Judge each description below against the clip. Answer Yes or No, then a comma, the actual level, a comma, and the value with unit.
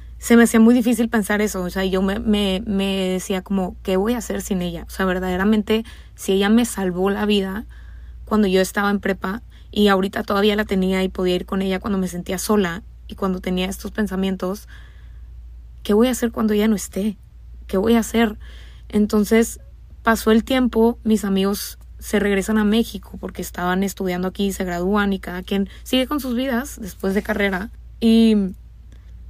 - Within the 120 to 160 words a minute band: No, fast, 190 wpm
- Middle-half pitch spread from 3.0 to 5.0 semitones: No, narrow, 2.5 semitones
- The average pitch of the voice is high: Yes, high, 200 Hz